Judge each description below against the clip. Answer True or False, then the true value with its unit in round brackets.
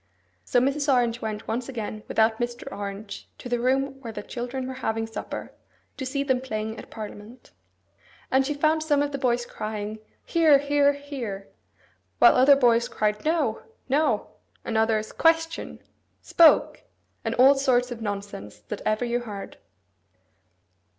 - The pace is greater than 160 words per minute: False (155 wpm)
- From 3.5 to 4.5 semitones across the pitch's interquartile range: True (4.1 semitones)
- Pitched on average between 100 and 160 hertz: False (245 Hz)